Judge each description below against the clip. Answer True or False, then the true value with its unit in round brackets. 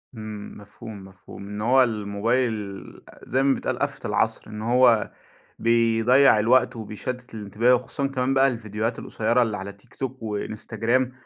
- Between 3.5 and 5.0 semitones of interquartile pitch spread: False (3.1 semitones)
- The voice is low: True (115 Hz)